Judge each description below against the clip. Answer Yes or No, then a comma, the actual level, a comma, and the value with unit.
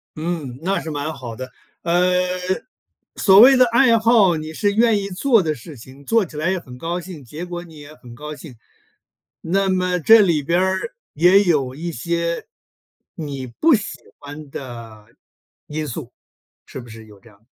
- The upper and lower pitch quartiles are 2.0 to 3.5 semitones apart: No, wide, 5.5 semitones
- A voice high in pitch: No, medium, 165 Hz